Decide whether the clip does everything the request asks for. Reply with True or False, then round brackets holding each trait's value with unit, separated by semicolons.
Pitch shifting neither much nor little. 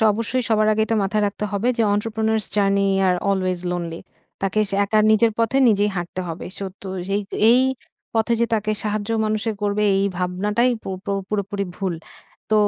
False (2.0 semitones)